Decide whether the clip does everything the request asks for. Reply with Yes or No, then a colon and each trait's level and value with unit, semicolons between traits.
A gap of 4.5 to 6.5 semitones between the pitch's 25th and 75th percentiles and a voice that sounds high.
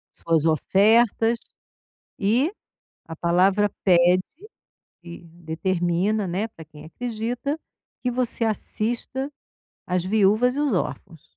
Yes: average, 5.2 semitones; high, 200 Hz